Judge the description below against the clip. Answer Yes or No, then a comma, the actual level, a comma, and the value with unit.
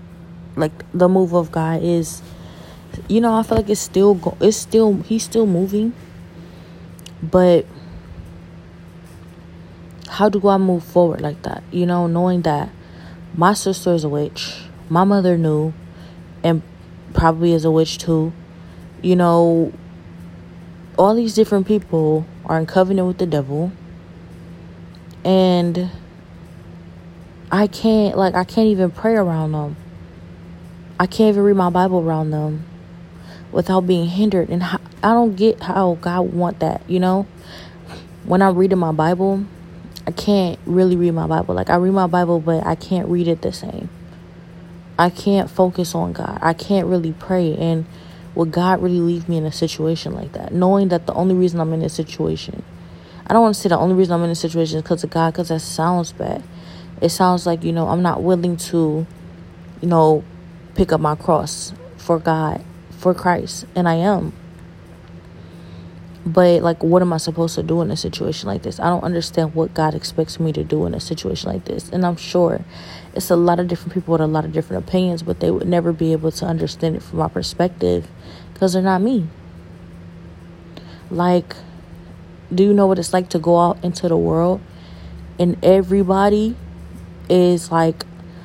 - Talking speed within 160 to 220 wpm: Yes, average, 175 wpm